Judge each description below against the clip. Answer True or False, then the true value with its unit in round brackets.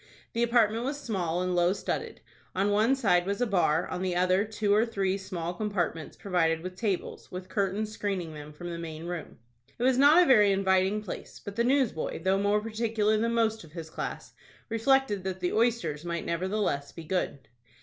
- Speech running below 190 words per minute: False (195 wpm)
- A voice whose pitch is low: False (195 Hz)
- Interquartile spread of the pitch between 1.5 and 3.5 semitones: False (3.9 semitones)